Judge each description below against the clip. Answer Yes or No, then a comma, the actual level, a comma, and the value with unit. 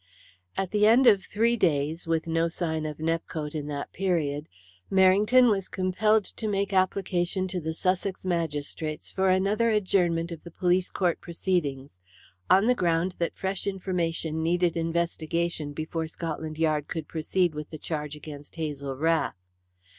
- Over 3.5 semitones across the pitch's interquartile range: No, average, 3.2 semitones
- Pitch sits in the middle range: Yes, medium, 170 Hz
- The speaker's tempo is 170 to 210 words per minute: No, average, 155 wpm